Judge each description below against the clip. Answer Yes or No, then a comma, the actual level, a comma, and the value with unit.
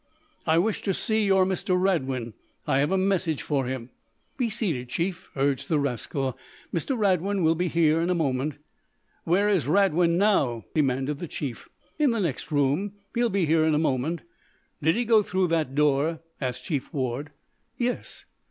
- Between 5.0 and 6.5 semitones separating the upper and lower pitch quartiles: Yes, wide, 5.6 semitones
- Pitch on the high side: No, medium, 165 Hz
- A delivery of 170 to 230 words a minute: Yes, average, 175 wpm